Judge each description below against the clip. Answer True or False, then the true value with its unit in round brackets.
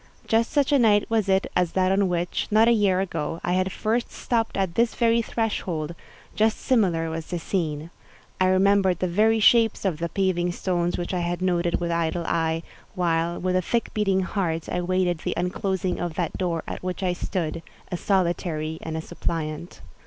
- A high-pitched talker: False (180 Hz)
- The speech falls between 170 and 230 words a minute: True (190 wpm)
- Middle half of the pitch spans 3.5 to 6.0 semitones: False (2.8 semitones)